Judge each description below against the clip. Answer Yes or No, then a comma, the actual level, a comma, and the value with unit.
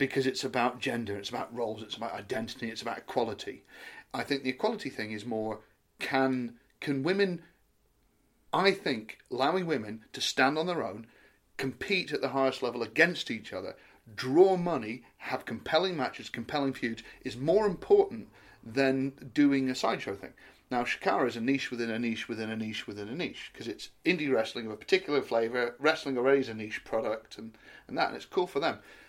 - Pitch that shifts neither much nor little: Yes, average, 3.4 semitones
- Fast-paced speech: No, average, 190 wpm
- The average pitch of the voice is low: Yes, low, 130 Hz